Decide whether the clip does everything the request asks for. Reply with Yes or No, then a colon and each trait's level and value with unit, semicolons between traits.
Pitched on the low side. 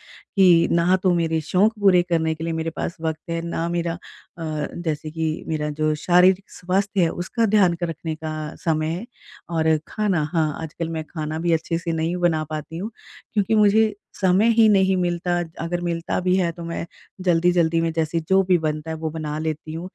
No: medium, 170 Hz